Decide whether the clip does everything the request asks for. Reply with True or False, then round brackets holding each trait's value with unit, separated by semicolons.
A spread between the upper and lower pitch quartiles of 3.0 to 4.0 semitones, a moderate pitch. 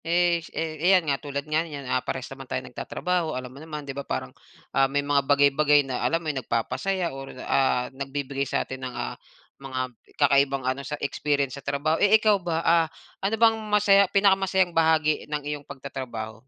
True (3.6 semitones; 145 Hz)